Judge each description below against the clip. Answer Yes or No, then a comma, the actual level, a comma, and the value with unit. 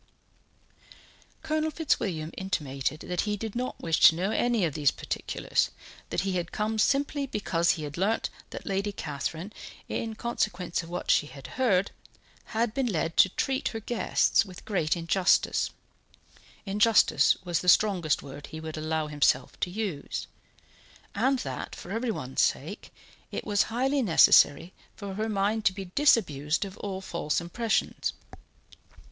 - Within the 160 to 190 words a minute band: No, average, 150 wpm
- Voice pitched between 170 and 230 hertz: Yes, high, 190 Hz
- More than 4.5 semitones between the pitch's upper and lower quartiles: Yes, average, 5.3 semitones